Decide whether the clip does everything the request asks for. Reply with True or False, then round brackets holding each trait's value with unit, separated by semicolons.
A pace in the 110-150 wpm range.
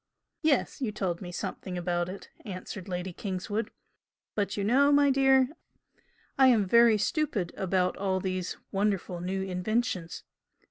True (140 wpm)